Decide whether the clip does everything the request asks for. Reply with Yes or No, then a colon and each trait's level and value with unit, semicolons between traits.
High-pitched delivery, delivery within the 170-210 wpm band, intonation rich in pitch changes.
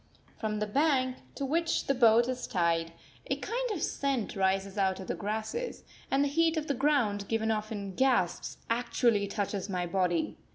Yes: high, 220 Hz; average, 180 wpm; wide, 5.7 semitones